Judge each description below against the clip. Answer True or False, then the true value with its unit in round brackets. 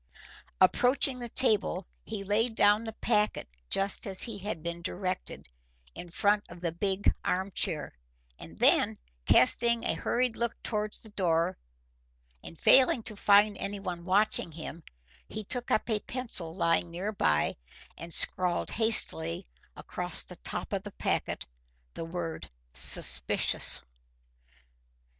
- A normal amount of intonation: True (4.2 semitones)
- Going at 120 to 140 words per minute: True (135 wpm)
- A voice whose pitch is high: True (200 Hz)